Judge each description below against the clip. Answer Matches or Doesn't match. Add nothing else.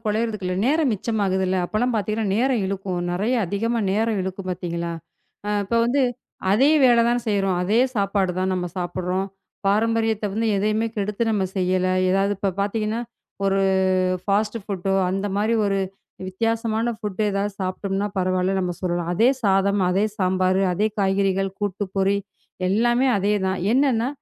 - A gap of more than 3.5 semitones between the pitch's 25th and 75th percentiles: Doesn't match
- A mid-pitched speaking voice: Doesn't match